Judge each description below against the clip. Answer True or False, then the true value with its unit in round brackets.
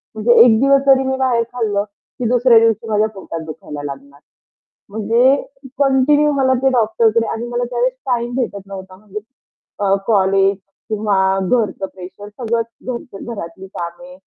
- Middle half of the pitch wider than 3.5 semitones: True (4.1 semitones)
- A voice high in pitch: True (225 Hz)